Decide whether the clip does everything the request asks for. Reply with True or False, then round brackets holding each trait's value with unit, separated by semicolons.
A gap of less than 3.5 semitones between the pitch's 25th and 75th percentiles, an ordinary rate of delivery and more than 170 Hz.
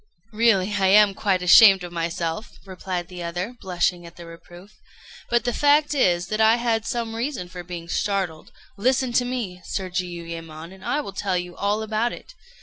False (4.2 semitones; 185 wpm; 190 Hz)